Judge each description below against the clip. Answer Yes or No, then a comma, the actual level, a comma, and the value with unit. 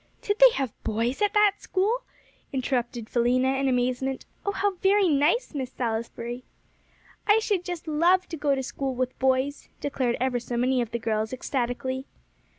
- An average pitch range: No, wide, 6.2 semitones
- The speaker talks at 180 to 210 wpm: No, average, 165 wpm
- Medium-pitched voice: No, very high, 265 Hz